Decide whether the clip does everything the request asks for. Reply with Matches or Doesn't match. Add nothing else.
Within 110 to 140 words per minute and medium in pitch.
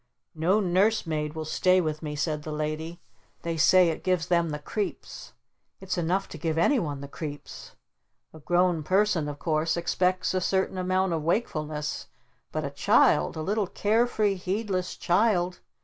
Doesn't match